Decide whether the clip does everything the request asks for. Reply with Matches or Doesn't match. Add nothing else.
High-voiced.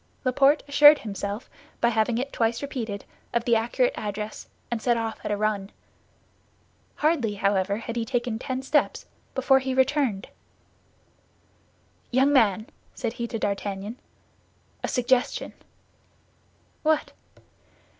Matches